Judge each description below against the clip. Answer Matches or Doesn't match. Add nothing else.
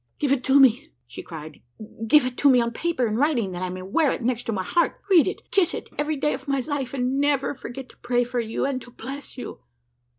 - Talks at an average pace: Doesn't match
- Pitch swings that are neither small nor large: Matches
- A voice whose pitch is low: Doesn't match